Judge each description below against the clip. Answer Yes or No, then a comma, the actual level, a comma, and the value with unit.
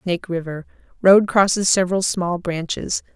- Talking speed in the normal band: No, slow, 115 wpm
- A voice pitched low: No, medium, 180 Hz